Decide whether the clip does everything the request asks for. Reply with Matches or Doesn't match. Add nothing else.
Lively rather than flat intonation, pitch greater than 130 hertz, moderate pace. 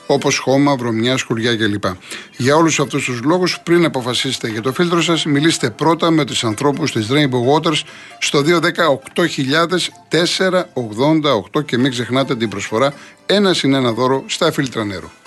Doesn't match